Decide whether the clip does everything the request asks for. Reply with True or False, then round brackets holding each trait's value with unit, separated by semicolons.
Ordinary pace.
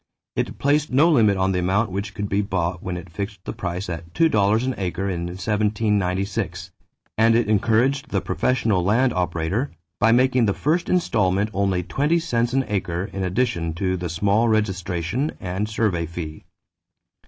True (165 wpm)